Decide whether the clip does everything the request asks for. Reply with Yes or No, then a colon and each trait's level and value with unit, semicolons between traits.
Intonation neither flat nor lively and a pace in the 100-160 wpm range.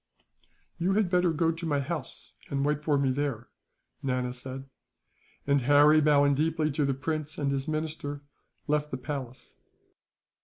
No: narrow, 2.2 semitones; average, 155 wpm